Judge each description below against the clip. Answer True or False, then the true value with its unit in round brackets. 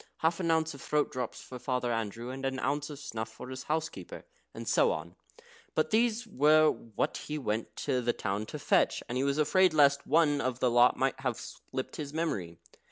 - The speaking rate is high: True (210 wpm)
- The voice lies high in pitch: False (135 Hz)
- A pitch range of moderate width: True (4.2 semitones)